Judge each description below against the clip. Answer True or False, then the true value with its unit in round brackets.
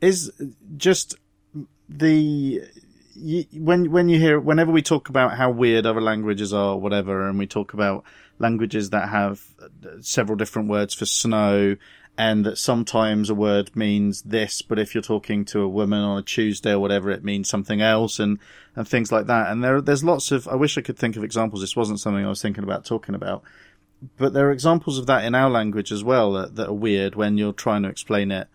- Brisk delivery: True (210 wpm)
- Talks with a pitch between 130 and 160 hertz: False (110 Hz)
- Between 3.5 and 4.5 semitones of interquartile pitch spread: True (4.2 semitones)